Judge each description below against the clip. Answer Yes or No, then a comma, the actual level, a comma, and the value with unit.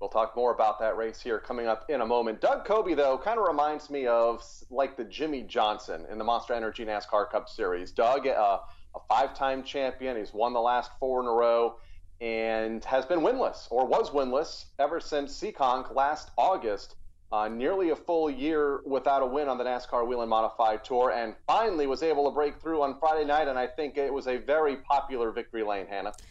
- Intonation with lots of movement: No, average, 4.0 semitones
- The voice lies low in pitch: Yes, low, 125 Hz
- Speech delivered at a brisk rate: Yes, fast, 210 wpm